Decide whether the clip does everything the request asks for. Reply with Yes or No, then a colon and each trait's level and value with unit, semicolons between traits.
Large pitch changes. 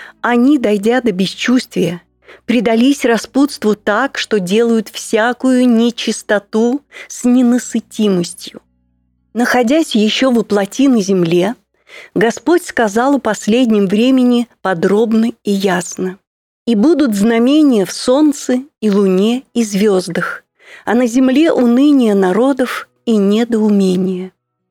No: average, 3.9 semitones